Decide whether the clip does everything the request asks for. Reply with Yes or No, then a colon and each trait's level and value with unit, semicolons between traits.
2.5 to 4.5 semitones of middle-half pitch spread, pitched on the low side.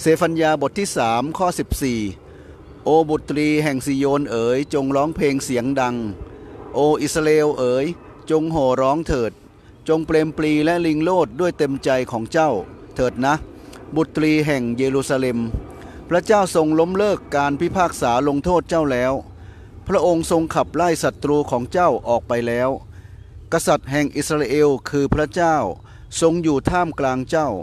No: average, 4.1 semitones; medium, 145 Hz